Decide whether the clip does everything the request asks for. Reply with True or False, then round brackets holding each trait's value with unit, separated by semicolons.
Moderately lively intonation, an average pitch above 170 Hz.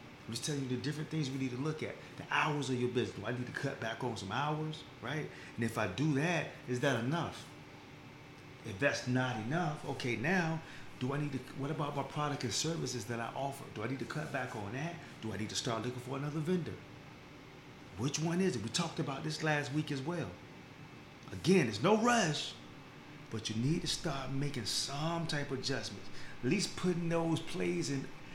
False (3.9 semitones; 140 Hz)